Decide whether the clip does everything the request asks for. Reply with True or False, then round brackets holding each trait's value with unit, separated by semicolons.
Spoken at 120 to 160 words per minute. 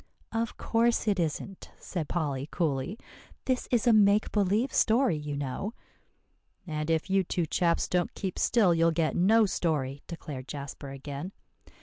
True (150 wpm)